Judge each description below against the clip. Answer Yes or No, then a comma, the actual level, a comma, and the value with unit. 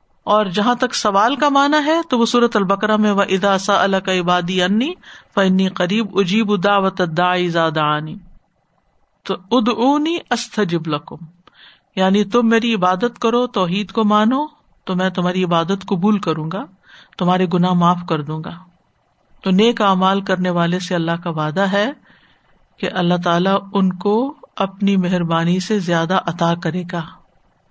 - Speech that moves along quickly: No, average, 155 wpm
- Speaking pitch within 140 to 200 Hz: Yes, high, 190 Hz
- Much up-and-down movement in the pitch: No, average, 3.1 semitones